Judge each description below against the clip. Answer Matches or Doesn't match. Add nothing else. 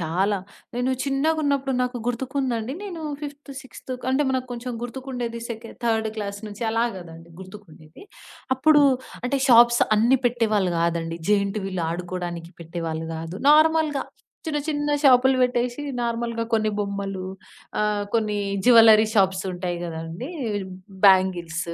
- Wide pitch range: Matches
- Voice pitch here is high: Matches